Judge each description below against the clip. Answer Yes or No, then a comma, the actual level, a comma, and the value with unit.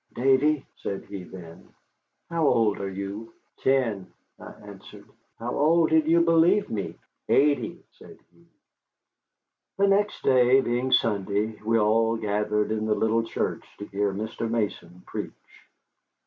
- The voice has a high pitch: No, low, 115 Hz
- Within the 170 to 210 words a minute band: No, slow, 135 wpm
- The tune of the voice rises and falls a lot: No, average, 4.8 semitones